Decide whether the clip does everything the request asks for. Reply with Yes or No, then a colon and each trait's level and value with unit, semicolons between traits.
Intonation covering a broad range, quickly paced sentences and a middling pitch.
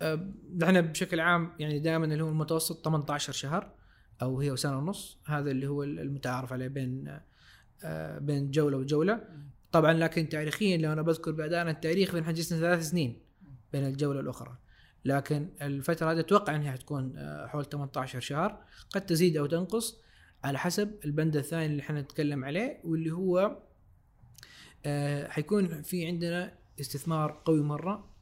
No: average, 3.3 semitones; fast, 140 wpm; medium, 155 Hz